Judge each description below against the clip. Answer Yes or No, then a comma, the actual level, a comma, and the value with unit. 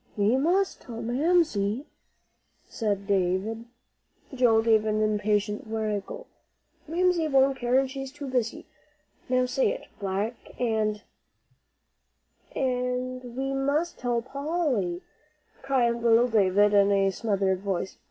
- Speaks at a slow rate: Yes, slow, 120 wpm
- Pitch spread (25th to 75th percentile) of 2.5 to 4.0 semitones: No, average, 4.4 semitones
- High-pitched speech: Yes, high, 235 Hz